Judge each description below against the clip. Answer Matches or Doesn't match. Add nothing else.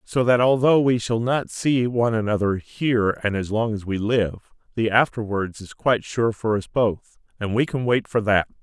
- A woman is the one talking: Doesn't match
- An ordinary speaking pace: Doesn't match